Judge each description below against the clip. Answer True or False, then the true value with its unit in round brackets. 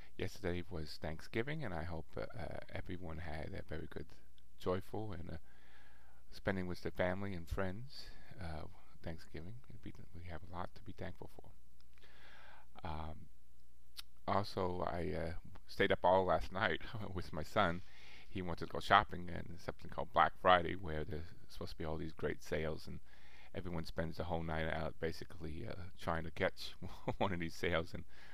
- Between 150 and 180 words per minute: True (170 wpm)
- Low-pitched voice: True (85 Hz)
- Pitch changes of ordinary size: True (3.4 semitones)